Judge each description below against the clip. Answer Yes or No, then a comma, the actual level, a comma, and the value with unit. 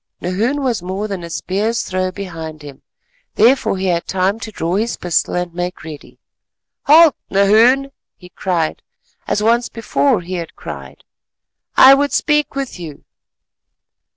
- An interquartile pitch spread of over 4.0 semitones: Yes, average, 5.1 semitones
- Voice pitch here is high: Yes, high, 195 Hz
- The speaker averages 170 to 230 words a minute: No, average, 150 wpm